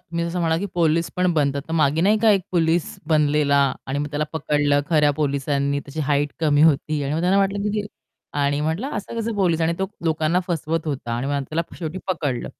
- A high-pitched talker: No, medium, 155 Hz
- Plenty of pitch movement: No, average, 3.2 semitones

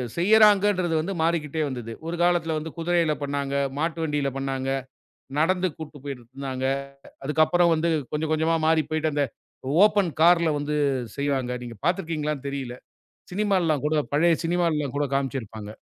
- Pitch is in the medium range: Yes, medium, 155 Hz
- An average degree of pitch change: Yes, average, 3.4 semitones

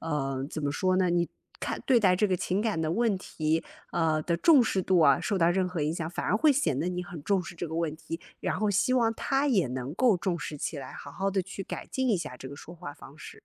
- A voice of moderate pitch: Yes, medium, 175 Hz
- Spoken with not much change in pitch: No, average, 4.2 semitones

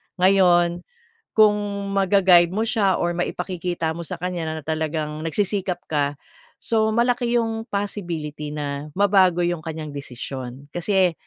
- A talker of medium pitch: Yes, medium, 175 Hz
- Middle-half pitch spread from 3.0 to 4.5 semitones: Yes, average, 4.0 semitones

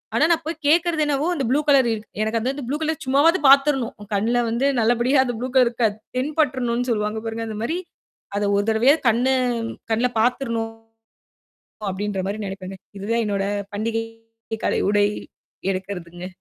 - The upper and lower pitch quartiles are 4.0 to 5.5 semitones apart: Yes, average, 4.5 semitones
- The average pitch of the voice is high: Yes, high, 235 Hz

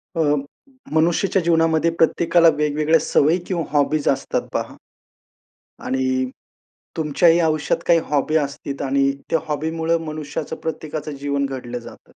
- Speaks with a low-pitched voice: No, medium, 155 Hz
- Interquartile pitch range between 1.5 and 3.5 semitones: Yes, narrow, 2.5 semitones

